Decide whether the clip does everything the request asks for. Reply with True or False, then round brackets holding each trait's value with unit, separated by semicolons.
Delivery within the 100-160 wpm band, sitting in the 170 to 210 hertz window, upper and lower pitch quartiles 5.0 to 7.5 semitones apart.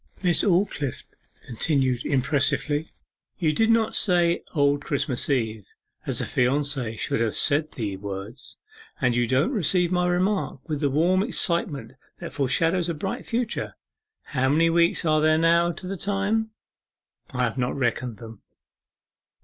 False (145 wpm; 150 Hz; 5.5 semitones)